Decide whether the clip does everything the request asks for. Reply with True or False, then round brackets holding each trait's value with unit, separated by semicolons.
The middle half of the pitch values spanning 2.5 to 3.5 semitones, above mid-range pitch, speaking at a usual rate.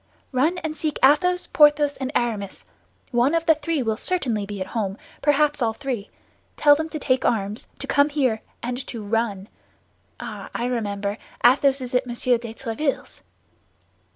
False (4.7 semitones; 255 Hz; 165 wpm)